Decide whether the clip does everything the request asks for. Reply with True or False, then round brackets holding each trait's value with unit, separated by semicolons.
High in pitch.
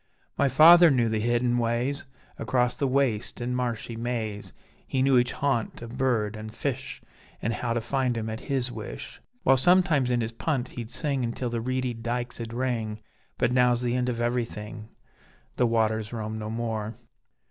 False (120 Hz)